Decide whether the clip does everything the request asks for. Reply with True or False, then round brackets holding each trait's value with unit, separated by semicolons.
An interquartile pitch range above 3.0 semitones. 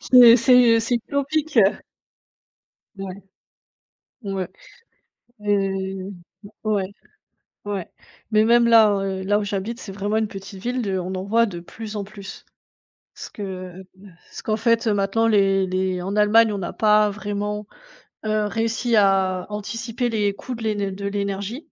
False (2.7 semitones)